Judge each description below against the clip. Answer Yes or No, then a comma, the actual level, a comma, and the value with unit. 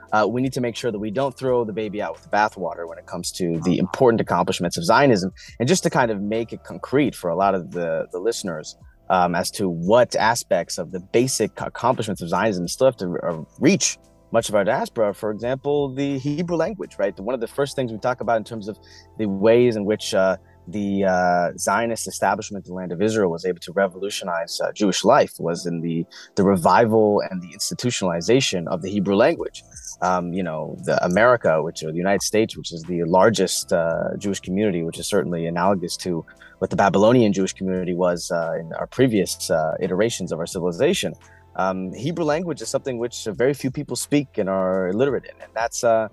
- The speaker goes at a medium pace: No, fast, 210 wpm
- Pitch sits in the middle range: No, low, 105 Hz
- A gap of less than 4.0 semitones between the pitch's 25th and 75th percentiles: No, average, 5.2 semitones